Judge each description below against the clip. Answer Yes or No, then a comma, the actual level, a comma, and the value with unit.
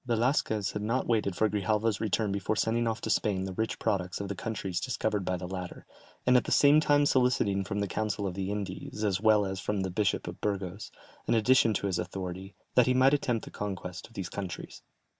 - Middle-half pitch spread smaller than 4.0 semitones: Yes, average, 2.9 semitones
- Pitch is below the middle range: Yes, low, 105 Hz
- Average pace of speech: No, fast, 220 wpm